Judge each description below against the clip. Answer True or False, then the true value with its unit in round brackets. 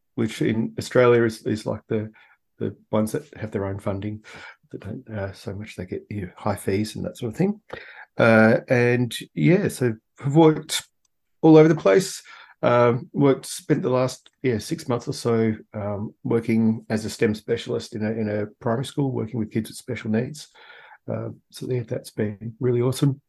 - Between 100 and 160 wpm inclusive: False (195 wpm)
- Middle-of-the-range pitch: False (115 Hz)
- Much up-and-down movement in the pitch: False (3.1 semitones)